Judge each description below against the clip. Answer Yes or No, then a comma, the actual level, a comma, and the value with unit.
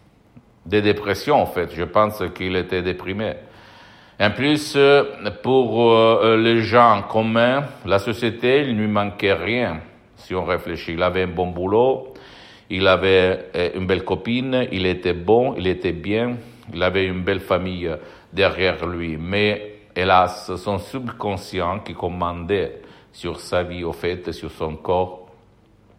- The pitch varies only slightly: No, average, 3.6 semitones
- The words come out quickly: No, average, 145 wpm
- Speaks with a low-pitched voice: Yes, low, 100 Hz